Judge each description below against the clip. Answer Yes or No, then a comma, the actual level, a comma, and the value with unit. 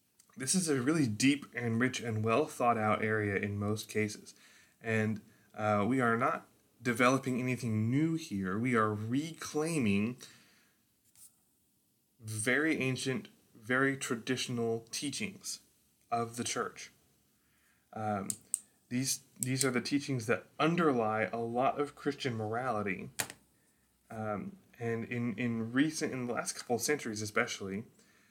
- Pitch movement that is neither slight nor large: Yes, average, 3.7 semitones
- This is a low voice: Yes, low, 120 Hz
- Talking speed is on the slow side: Yes, slow, 125 wpm